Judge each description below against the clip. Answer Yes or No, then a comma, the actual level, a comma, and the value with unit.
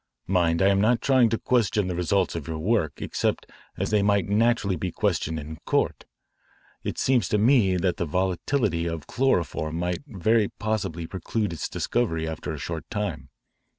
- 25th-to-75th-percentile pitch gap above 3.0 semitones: Yes, average, 4.7 semitones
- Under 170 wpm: No, average, 175 wpm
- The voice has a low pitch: Yes, very low, 95 Hz